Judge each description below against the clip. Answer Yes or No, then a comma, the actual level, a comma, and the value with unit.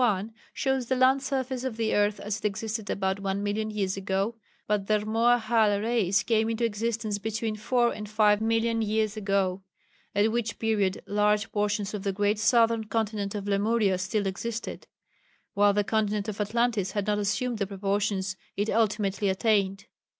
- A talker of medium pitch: No, high, 210 Hz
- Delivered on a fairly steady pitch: Yes, narrow, 2.0 semitones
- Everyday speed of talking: Yes, average, 170 wpm